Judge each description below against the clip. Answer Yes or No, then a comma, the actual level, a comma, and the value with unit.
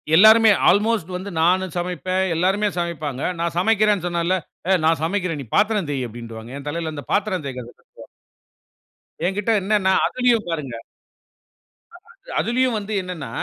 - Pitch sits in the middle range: Yes, medium, 180 Hz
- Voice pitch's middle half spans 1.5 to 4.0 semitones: No, average, 4.8 semitones